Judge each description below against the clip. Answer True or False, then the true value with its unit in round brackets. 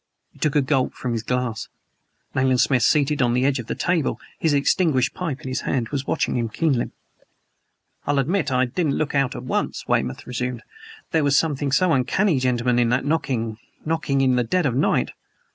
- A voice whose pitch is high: False (135 Hz)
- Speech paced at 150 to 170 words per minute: False (200 wpm)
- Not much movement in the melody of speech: False (3.2 semitones)